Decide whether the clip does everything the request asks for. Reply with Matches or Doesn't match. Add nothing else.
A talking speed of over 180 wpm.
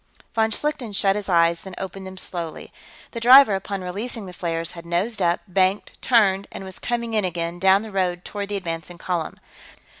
Matches